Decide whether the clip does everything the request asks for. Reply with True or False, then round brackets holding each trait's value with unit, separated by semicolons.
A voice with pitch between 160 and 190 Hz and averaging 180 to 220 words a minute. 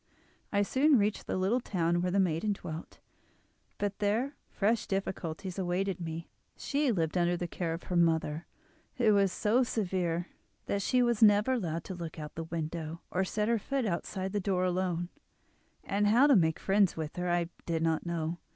True (185 Hz; 190 wpm)